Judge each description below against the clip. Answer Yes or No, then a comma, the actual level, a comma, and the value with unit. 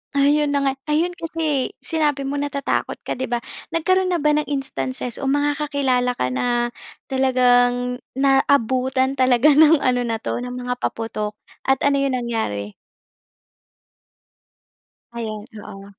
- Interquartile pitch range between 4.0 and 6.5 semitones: No, average, 2.7 semitones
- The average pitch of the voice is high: Yes, very high, 265 Hz